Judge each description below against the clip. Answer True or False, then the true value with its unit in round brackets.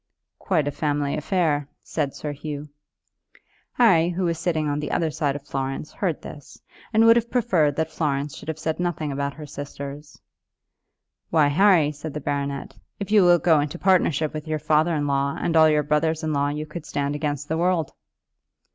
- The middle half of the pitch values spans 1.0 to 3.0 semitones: True (2.5 semitones)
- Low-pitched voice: False (150 Hz)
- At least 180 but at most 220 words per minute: True (190 wpm)